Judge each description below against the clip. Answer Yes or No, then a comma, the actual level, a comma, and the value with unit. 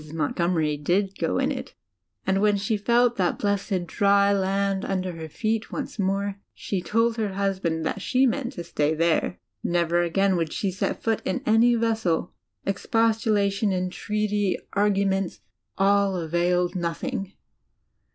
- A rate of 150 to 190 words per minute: No, average, 140 wpm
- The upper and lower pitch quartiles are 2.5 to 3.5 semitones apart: Yes, average, 2.9 semitones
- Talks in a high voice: Yes, high, 195 Hz